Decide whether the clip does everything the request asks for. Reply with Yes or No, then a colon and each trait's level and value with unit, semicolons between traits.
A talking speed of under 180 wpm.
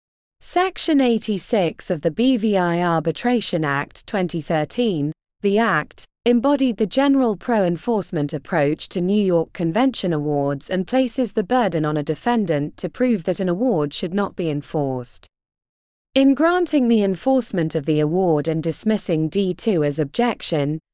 Yes: average, 140 wpm